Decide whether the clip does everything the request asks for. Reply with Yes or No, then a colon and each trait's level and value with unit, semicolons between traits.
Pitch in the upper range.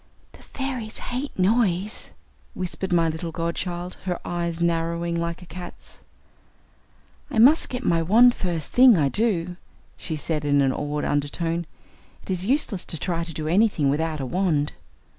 No: medium, 170 Hz